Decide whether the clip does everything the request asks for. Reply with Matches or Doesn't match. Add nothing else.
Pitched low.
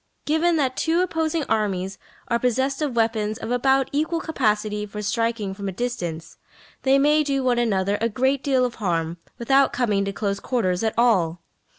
Doesn't match